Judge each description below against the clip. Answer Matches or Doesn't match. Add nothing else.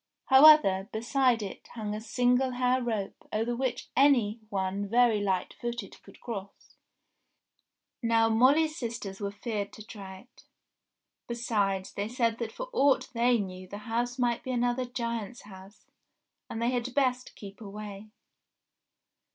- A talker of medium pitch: Doesn't match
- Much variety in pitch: Doesn't match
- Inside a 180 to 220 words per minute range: Doesn't match